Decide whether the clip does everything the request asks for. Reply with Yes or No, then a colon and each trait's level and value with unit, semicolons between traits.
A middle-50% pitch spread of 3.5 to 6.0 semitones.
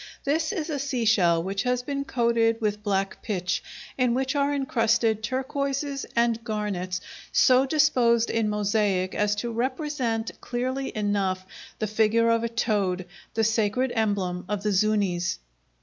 Yes: average, 3.9 semitones